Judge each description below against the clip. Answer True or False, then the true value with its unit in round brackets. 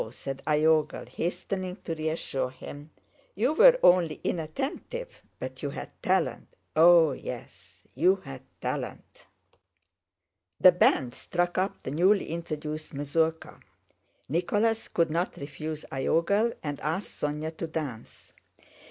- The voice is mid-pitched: True (160 Hz)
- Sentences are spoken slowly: True (115 wpm)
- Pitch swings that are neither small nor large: True (3.6 semitones)